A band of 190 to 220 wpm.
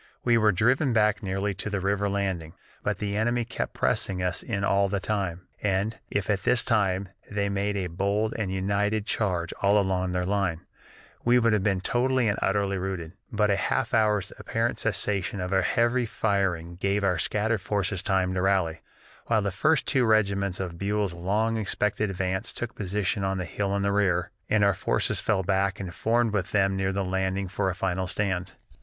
Yes: average, 195 wpm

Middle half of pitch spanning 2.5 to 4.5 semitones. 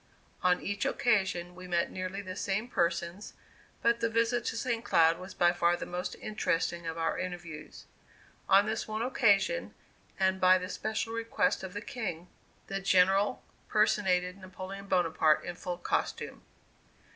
Yes: average, 3.4 semitones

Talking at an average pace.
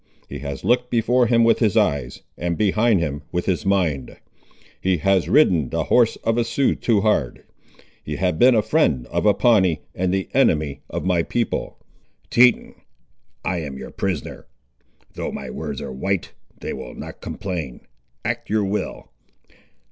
Yes: average, 165 wpm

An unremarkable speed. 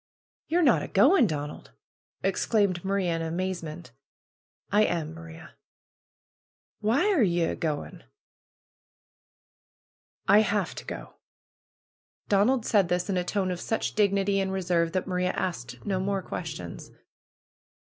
No: slow, 130 wpm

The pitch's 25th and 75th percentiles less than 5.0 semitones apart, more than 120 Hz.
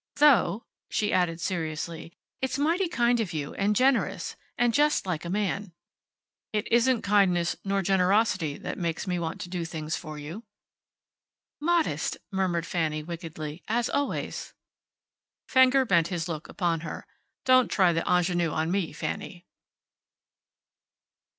No: wide, 5.5 semitones; medium, 185 Hz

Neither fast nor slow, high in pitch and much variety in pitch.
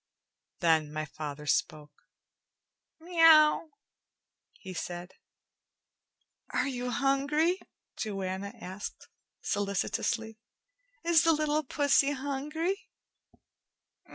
No: slow, 75 wpm; very high, 250 Hz; wide, 8.7 semitones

